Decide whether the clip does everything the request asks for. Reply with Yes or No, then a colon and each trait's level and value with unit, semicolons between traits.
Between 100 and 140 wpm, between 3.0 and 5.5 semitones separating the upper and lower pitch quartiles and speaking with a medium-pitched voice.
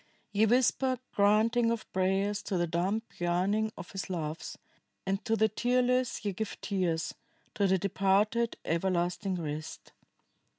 No: slow, 135 wpm; average, 3.5 semitones; high, 200 Hz